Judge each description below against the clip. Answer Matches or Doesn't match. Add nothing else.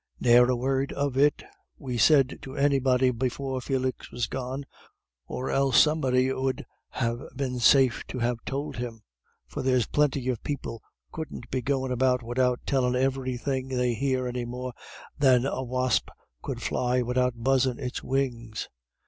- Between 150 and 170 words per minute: Matches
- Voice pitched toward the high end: Doesn't match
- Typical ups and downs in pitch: Doesn't match